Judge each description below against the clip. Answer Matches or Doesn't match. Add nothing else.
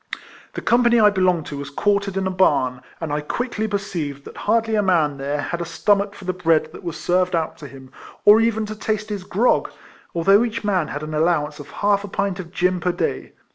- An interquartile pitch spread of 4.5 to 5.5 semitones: Matches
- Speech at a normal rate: Doesn't match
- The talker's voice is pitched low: Doesn't match